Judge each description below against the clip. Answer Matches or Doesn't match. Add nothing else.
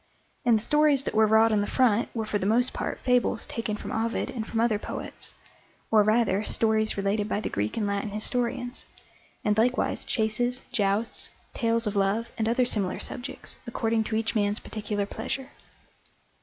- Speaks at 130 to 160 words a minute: Doesn't match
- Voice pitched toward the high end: Matches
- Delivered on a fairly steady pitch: Matches